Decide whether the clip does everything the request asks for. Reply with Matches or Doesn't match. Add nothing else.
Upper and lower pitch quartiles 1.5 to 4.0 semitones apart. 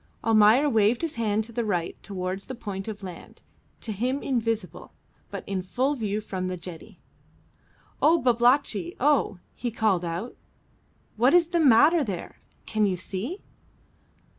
Doesn't match